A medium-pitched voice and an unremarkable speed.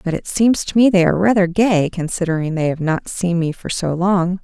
No: medium, 180 Hz; fast, 245 wpm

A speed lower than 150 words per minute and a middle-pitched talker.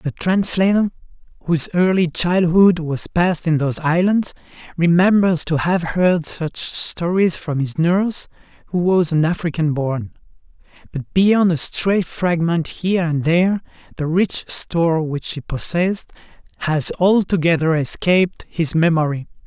Yes: slow, 135 wpm; medium, 170 Hz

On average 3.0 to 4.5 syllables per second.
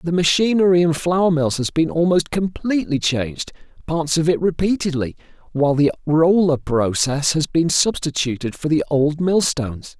No: 4.9 syllables/s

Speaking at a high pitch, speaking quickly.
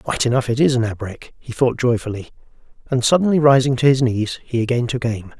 No: low, 125 Hz; fast, 210 wpm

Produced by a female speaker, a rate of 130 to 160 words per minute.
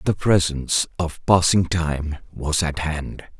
No: male; average, 140 wpm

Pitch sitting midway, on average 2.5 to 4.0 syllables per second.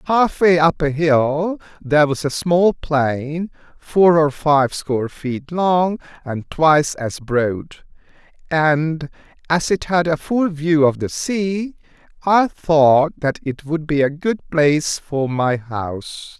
Yes: medium, 155 Hz; 3.4 syllables/s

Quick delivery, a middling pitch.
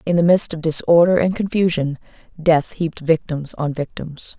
No: average, 165 wpm; medium, 165 Hz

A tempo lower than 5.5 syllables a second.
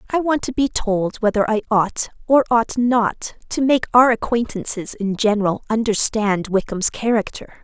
Yes: 4.5 syllables/s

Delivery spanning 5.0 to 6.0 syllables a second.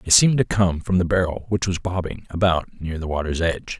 Yes: 5.8 syllables/s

